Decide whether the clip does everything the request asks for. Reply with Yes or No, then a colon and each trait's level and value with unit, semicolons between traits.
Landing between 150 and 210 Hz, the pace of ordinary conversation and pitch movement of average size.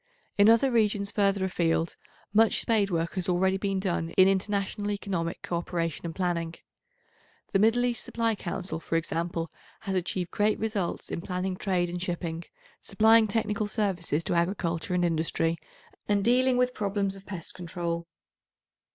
Yes: high, 190 Hz; average, 160 wpm; average, 3.4 semitones